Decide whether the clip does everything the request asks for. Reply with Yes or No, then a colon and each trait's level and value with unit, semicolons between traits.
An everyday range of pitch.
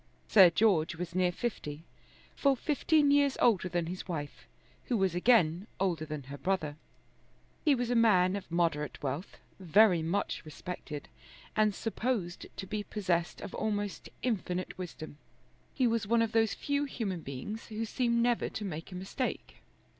Yes: average, 5.0 semitones